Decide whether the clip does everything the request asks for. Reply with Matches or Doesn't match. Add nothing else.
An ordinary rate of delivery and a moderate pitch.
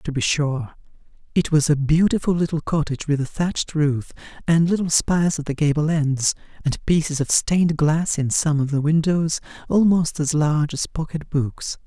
Matches